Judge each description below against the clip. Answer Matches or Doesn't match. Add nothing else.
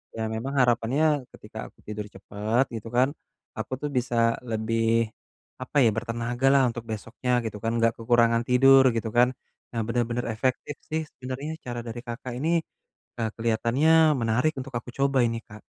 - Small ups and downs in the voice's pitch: Matches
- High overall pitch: Doesn't match